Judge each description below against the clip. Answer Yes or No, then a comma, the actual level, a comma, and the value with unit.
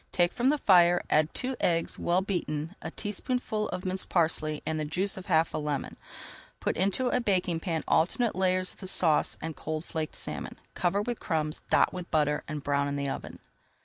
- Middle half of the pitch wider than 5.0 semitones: No, average, 3.7 semitones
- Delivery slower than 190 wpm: No, average, 200 wpm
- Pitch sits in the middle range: Yes, medium, 175 Hz